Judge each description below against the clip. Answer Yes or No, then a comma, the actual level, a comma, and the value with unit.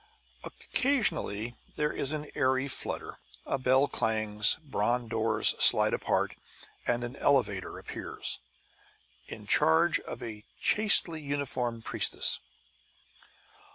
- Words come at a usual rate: No, slow, 105 wpm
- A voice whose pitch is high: No, low, 125 Hz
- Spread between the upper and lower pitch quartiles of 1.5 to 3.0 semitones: No, average, 4.2 semitones